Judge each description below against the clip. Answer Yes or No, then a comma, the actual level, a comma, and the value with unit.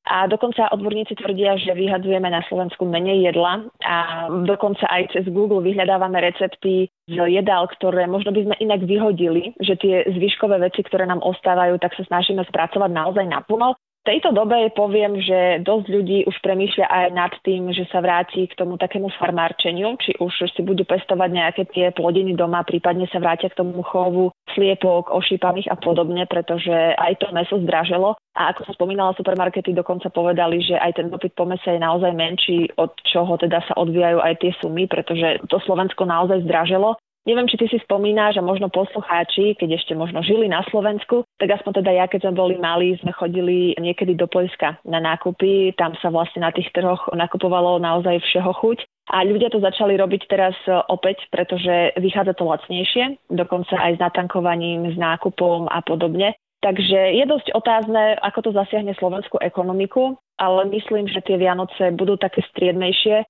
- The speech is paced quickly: Yes, fast, 175 wpm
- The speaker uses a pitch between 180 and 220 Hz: Yes, medium, 185 Hz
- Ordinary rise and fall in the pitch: No, narrow, 2.1 semitones